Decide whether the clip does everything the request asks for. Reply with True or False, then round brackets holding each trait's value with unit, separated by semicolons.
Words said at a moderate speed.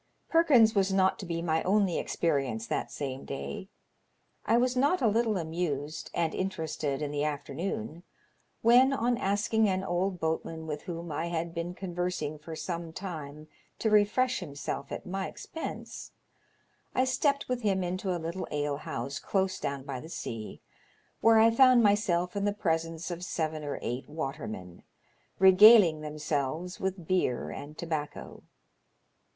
True (150 wpm)